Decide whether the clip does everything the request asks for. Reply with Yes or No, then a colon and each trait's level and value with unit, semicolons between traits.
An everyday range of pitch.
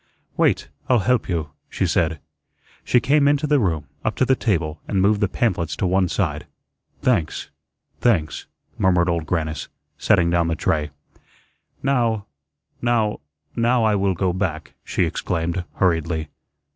No: wide, 6.0 semitones